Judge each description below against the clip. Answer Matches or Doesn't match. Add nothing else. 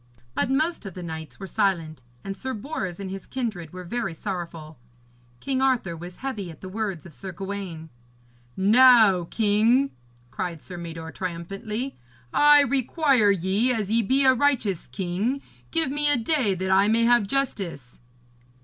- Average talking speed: Matches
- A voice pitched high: Matches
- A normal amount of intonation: Doesn't match